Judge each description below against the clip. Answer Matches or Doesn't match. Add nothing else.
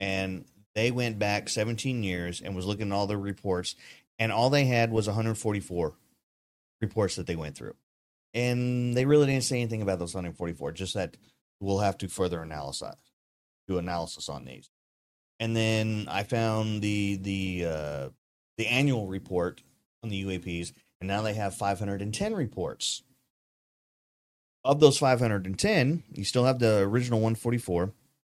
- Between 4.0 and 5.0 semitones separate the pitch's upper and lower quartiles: Matches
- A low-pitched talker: Matches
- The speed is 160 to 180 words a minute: Doesn't match